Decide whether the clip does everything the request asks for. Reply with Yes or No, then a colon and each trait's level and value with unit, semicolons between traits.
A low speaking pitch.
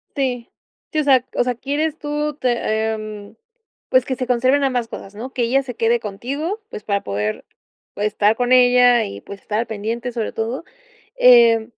No: high, 240 Hz